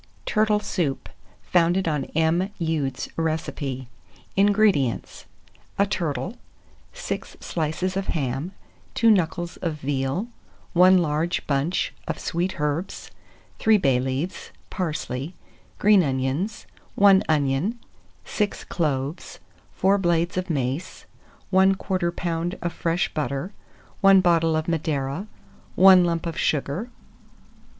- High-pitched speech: No, medium, 170 Hz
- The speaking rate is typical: No, slow, 110 wpm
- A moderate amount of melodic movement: Yes, average, 4.3 semitones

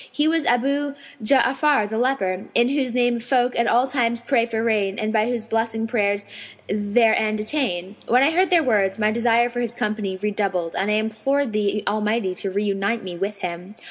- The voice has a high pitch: Yes, high, 225 Hz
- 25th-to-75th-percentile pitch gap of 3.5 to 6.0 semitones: No, average, 3.1 semitones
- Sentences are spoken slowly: No, average, 195 wpm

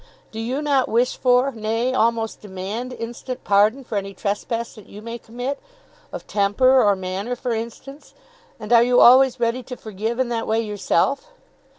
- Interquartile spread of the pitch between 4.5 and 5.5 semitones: No, average, 2.9 semitones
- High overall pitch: Yes, high, 230 Hz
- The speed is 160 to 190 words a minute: Yes, average, 175 wpm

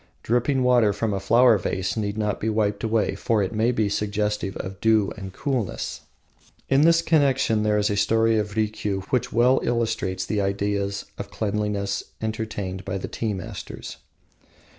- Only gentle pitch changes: Yes, narrow, 2.2 semitones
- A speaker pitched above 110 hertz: No, low, 105 Hz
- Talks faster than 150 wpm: Yes, average, 165 wpm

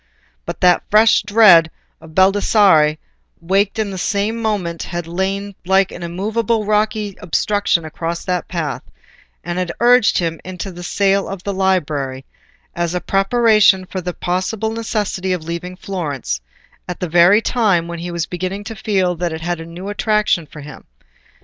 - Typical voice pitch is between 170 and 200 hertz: Yes, medium, 185 Hz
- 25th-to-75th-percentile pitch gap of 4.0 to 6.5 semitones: No, average, 3.2 semitones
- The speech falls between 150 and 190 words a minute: Yes, average, 165 wpm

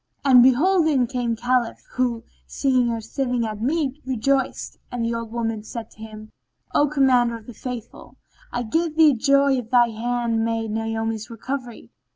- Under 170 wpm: No, average, 175 wpm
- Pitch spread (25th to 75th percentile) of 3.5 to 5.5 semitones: No, average, 2.8 semitones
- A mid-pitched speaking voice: No, high, 240 Hz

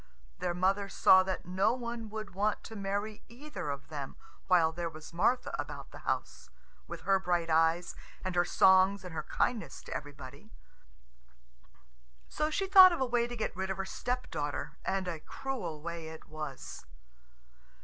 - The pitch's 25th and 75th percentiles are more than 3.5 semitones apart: Yes, average, 5.1 semitones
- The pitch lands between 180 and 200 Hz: Yes, high, 190 Hz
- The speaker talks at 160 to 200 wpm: Yes, average, 170 wpm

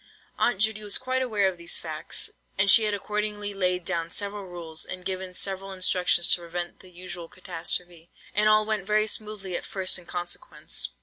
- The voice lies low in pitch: No, high, 190 Hz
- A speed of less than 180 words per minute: No, average, 185 wpm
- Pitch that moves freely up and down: No, average, 2.9 semitones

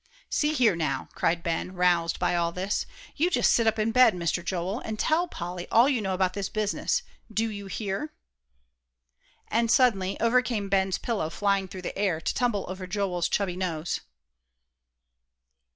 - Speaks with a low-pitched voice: No, high, 195 Hz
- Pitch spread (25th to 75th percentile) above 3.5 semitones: Yes, average, 4.0 semitones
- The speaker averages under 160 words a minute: No, average, 170 wpm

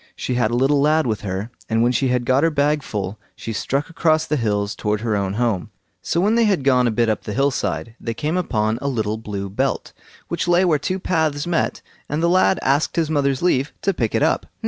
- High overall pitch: No, low, 130 Hz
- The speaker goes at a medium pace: No, fast, 240 wpm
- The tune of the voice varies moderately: No, wide, 6.2 semitones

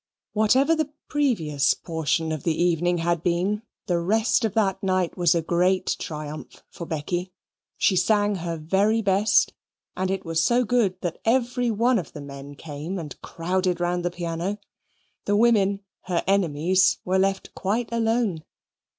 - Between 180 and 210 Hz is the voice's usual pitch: Yes, medium, 185 Hz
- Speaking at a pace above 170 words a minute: No, average, 160 wpm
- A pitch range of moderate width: Yes, average, 3.9 semitones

